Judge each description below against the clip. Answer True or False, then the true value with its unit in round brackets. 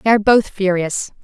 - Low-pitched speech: False (200 Hz)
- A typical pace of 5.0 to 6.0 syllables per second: True (5.9 syllables/s)